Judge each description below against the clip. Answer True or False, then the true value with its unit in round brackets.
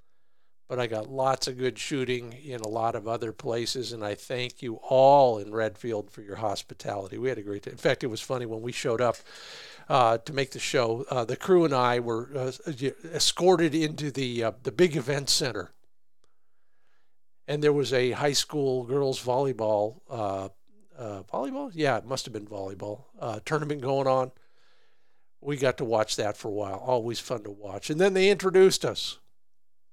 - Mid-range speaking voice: False (125 Hz)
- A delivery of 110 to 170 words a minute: False (190 wpm)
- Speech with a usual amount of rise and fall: True (3.8 semitones)